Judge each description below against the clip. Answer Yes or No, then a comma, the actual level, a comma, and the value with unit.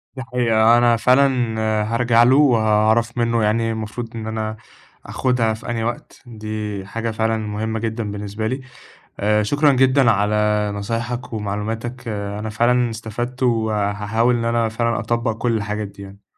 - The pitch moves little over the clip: Yes, narrow, 1.9 semitones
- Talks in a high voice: No, low, 115 Hz